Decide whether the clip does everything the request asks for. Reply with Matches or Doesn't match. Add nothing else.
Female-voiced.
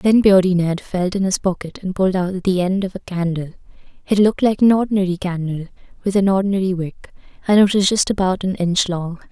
Matches